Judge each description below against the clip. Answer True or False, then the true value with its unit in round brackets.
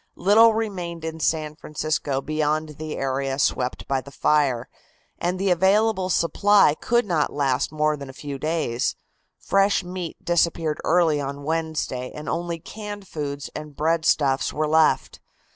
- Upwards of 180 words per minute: False (145 wpm)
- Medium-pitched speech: True (155 Hz)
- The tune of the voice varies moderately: True (3.6 semitones)